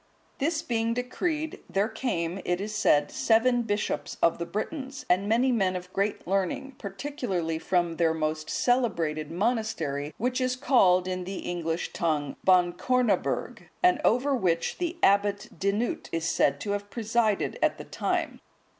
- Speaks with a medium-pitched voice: No, high, 200 Hz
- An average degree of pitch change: No, wide, 6.0 semitones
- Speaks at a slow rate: No, average, 150 wpm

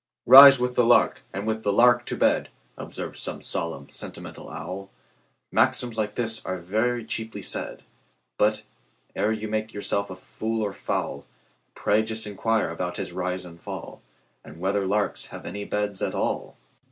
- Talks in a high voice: No, low, 105 Hz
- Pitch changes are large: No, average, 2.8 semitones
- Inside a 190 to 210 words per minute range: No, average, 150 wpm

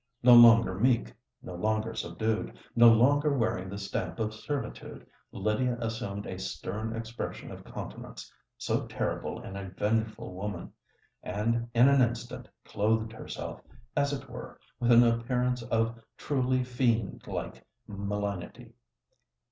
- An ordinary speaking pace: No, slow, 120 wpm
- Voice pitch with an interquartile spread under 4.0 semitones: Yes, average, 2.8 semitones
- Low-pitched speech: Yes, low, 115 Hz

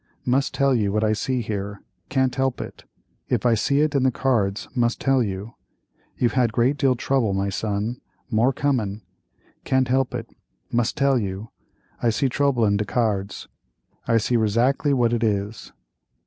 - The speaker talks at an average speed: Yes, average, 165 wpm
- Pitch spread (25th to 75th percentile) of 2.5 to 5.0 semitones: Yes, average, 3.9 semitones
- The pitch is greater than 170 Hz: No, low, 120 Hz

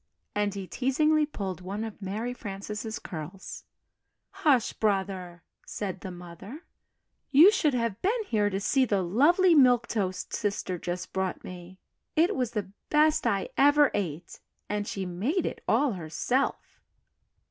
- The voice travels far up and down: Yes, wide, 6.1 semitones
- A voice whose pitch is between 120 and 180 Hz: No, high, 210 Hz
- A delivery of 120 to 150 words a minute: Yes, average, 145 wpm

